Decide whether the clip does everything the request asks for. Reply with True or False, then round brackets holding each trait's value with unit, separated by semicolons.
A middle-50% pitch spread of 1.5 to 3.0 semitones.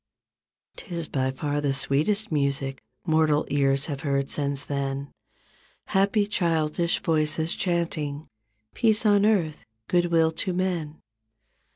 False (3.7 semitones)